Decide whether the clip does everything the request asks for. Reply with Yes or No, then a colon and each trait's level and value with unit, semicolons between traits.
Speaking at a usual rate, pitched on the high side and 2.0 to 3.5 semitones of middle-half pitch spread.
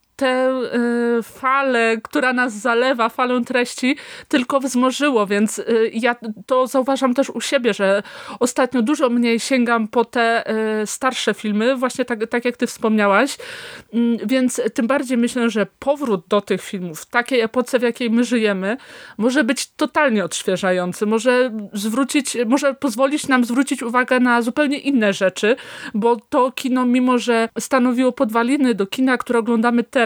Yes: average, 145 wpm; high, 245 Hz; narrow, 2.6 semitones